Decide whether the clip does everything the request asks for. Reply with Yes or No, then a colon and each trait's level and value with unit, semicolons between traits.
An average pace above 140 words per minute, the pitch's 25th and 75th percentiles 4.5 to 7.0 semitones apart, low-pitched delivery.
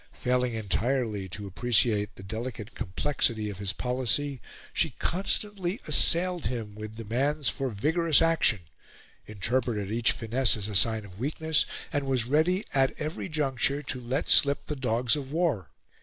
Yes: average, 150 wpm; average, 5.3 semitones; low, 125 Hz